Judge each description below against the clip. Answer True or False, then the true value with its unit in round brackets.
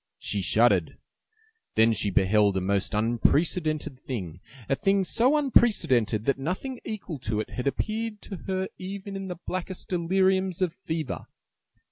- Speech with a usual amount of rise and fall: False (8.6 semitones)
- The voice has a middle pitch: True (170 Hz)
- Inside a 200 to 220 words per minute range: False (145 wpm)